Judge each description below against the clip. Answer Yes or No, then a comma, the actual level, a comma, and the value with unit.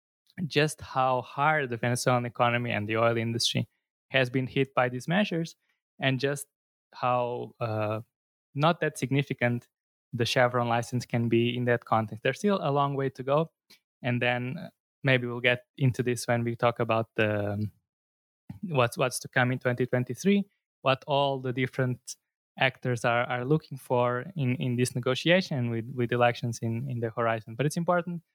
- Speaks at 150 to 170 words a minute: Yes, average, 165 wpm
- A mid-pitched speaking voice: No, low, 125 Hz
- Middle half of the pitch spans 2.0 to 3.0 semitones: Yes, narrow, 2.6 semitones